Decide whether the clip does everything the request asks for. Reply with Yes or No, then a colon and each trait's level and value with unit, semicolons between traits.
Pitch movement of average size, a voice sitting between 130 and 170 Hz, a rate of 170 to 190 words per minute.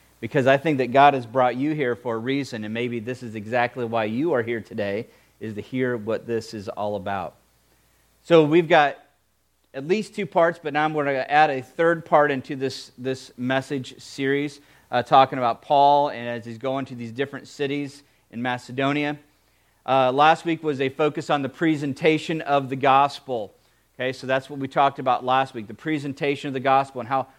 No: average, 3.2 semitones; low, 135 Hz; fast, 205 wpm